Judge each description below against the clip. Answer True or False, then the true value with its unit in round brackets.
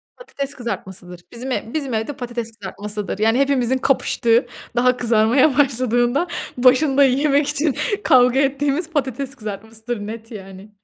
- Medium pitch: False (245 Hz)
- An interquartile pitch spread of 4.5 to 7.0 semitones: False (3.8 semitones)